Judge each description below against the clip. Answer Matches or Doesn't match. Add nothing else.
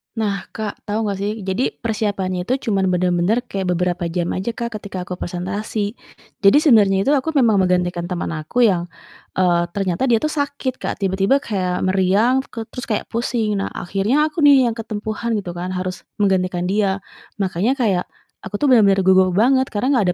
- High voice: Matches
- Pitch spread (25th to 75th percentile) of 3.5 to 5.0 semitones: Matches